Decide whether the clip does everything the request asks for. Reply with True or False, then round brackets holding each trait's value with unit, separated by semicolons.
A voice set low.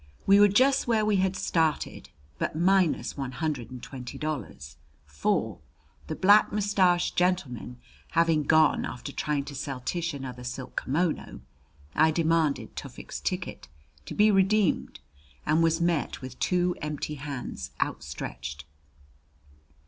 False (155 Hz)